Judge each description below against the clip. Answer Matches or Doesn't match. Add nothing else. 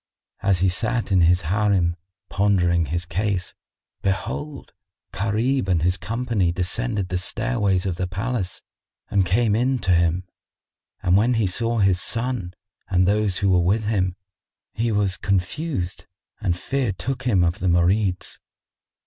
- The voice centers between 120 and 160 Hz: Doesn't match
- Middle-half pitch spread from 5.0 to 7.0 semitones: Doesn't match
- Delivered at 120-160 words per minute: Matches